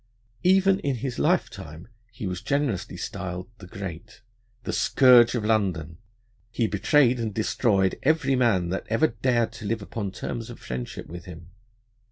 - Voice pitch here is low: Yes, low, 110 Hz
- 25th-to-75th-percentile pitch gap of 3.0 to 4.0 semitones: No, average, 5.1 semitones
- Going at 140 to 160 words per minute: Yes, average, 155 wpm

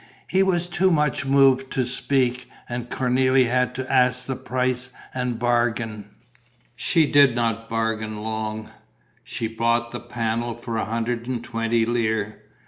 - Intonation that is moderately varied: No, narrow, 2.2 semitones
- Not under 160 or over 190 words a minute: No, average, 145 wpm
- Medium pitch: No, low, 120 Hz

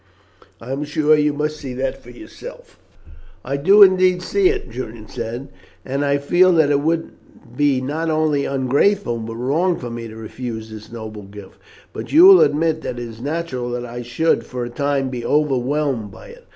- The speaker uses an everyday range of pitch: Yes, average, 4.6 semitones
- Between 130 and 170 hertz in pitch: Yes, medium, 140 Hz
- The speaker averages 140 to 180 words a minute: No, average, 190 wpm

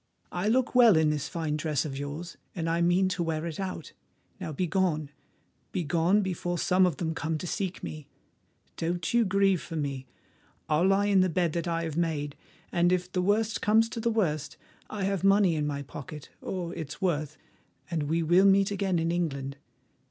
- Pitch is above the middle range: No, medium, 170 Hz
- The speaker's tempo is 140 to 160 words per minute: No, average, 185 wpm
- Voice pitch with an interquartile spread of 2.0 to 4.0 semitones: Yes, average, 3.6 semitones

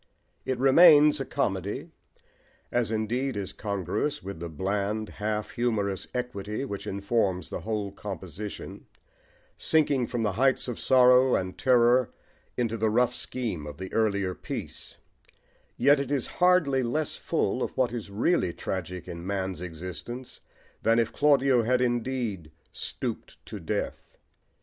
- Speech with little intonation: No, average, 4.7 semitones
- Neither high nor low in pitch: No, low, 115 Hz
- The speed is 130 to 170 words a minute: Yes, average, 140 wpm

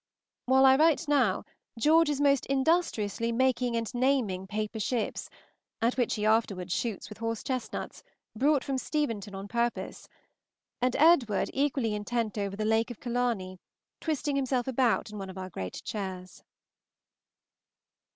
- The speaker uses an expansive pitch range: No, average, 4.2 semitones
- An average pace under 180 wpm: Yes, average, 145 wpm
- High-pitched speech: Yes, high, 235 Hz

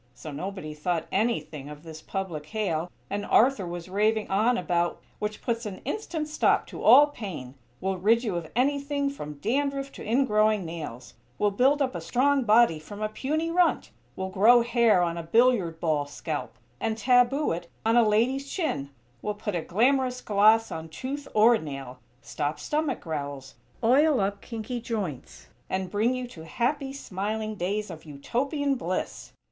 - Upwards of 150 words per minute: Yes, average, 170 wpm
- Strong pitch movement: Yes, wide, 6.6 semitones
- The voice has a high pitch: Yes, high, 215 Hz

